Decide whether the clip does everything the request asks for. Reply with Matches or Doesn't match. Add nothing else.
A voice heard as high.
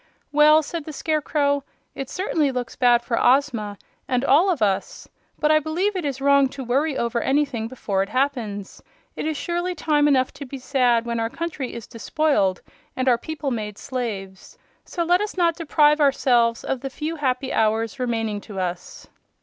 Matches